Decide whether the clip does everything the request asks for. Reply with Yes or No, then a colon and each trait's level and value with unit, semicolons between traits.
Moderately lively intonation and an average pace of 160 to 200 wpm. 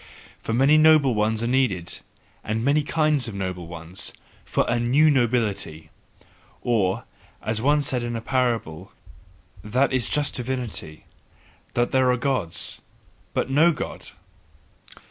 No: average, 4.3 semitones; slow, 135 wpm